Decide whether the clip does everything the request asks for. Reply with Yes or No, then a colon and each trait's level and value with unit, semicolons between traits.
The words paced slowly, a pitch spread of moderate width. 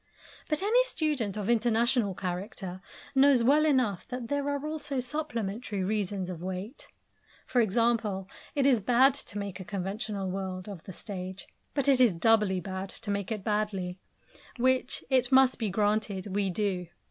No: average, 160 wpm; average, 5.0 semitones